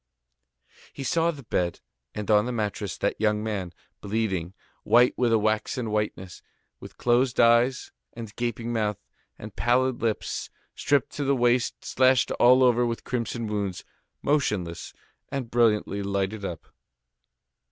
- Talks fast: No, average, 140 wpm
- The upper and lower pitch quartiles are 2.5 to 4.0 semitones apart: Yes, average, 3.0 semitones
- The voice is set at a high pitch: No, low, 115 Hz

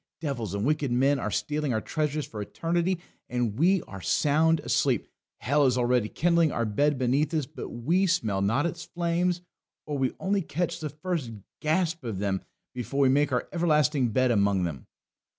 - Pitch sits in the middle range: Yes, medium, 145 Hz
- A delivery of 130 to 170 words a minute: No, average, 180 wpm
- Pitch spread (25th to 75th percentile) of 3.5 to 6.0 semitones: Yes, average, 5.3 semitones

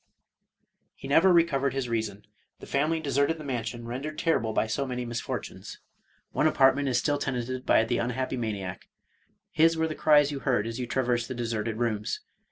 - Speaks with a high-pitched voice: No, low, 130 Hz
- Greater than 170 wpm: Yes, average, 185 wpm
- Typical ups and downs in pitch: Yes, average, 3.6 semitones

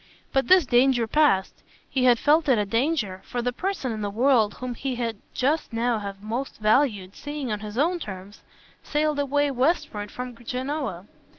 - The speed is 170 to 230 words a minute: Yes, average, 180 wpm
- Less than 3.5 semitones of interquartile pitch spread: No, average, 5.1 semitones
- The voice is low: No, high, 245 Hz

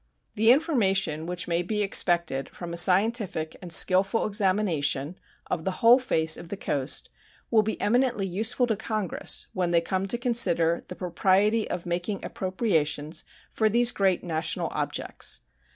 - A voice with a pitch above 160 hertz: Yes, high, 190 Hz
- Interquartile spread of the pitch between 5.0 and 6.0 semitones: No, average, 4.2 semitones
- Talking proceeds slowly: No, average, 150 wpm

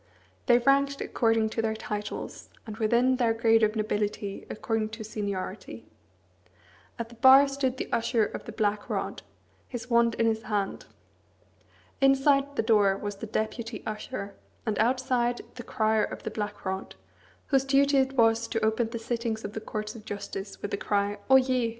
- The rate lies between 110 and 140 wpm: No, average, 170 wpm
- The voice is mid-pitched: No, high, 225 Hz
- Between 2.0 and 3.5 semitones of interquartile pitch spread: Yes, average, 2.9 semitones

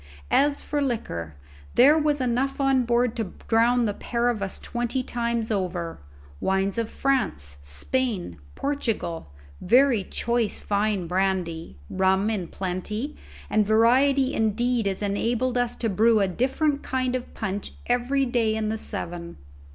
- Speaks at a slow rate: No, average, 145 wpm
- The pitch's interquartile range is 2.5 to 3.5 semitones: No, average, 4.6 semitones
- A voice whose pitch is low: No, high, 230 Hz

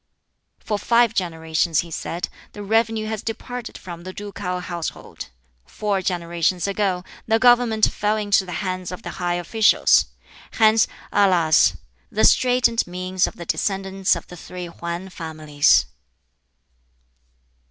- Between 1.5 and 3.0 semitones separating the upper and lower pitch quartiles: No, average, 3.9 semitones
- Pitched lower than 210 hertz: Yes, medium, 185 Hz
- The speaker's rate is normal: No, slow, 130 wpm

